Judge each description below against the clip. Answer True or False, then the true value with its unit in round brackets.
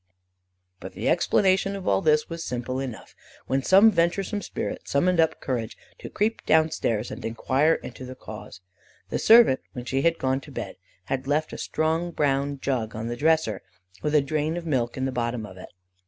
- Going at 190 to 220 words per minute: True (195 wpm)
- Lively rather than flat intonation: False (4.6 semitones)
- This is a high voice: False (140 Hz)